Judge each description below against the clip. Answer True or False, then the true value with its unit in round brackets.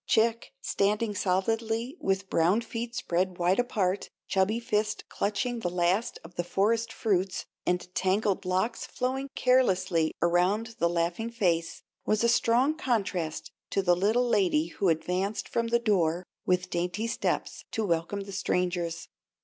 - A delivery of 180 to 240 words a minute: False (145 wpm)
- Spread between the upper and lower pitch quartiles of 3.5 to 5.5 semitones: True (4.2 semitones)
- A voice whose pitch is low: False (195 Hz)